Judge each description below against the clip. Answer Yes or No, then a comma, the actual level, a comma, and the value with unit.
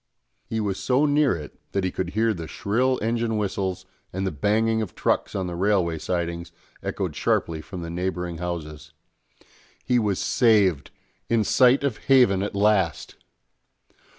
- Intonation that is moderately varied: Yes, average, 4.4 semitones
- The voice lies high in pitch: No, low, 100 Hz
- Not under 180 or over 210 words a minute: No, average, 155 wpm